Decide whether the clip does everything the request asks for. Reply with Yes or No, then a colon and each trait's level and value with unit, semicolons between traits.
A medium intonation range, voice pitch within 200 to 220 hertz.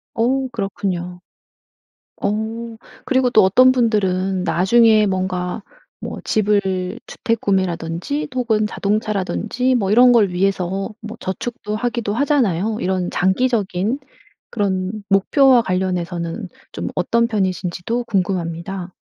Yes: average, 4.0 semitones; high, 205 Hz